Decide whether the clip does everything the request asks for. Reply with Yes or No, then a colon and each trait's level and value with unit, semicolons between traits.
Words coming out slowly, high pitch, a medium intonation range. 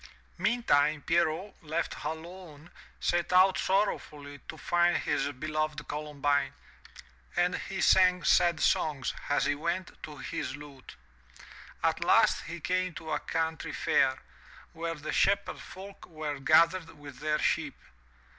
No: slow, 130 wpm; medium, 160 Hz; average, 3.2 semitones